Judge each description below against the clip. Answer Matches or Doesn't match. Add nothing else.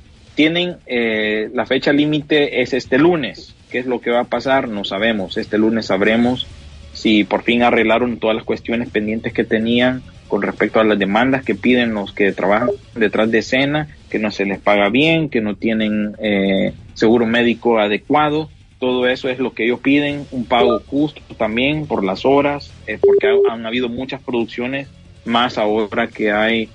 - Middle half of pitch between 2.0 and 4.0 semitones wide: Matches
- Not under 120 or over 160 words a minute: Doesn't match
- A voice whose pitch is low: Matches